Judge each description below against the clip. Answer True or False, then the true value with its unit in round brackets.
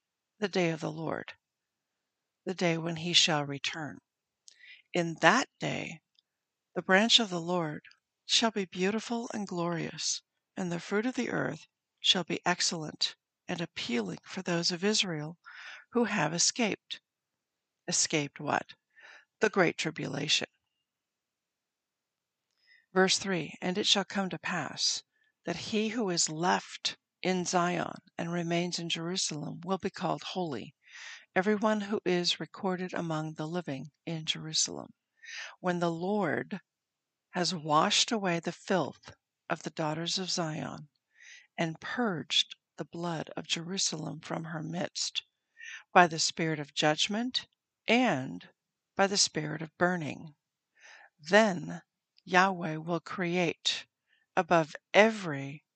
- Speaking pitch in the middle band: True (175 Hz)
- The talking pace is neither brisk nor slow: False (125 wpm)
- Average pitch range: True (3.3 semitones)